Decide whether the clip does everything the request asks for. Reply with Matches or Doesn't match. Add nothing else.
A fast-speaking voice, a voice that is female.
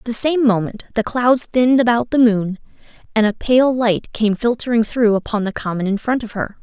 Matches